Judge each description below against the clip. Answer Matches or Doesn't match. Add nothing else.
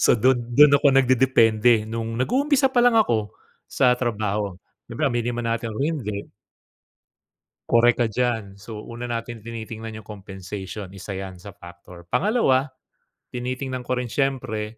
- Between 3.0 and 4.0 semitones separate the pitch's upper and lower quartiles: Matches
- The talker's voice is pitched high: Doesn't match